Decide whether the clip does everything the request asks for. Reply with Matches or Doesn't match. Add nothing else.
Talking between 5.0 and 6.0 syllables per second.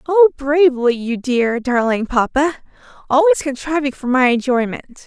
Doesn't match